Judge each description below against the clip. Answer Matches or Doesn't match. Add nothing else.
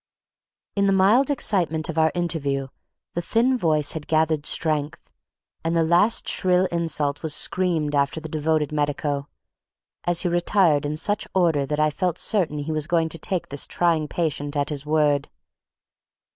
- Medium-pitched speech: Matches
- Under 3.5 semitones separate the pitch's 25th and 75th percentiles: Matches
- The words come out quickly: Doesn't match